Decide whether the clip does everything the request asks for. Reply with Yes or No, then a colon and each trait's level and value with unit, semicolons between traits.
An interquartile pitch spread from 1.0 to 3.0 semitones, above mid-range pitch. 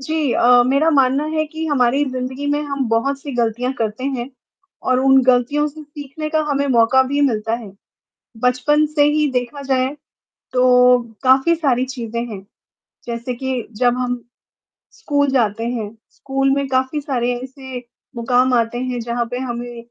Yes: narrow, 2.5 semitones; very high, 255 Hz